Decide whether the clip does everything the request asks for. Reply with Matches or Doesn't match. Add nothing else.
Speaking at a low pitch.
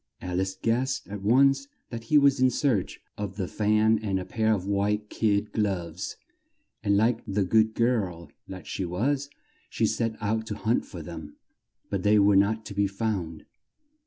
Matches